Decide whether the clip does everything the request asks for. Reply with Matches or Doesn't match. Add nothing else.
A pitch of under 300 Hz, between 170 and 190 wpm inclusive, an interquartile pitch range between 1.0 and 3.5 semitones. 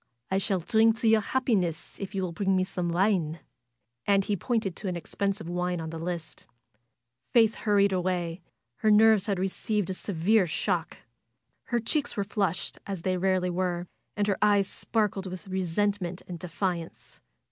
Matches